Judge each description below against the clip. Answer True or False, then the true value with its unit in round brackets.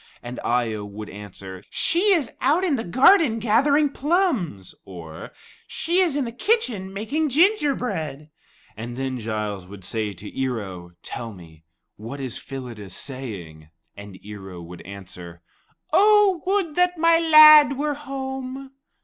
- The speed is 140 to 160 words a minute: True (150 wpm)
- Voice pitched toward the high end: False (155 Hz)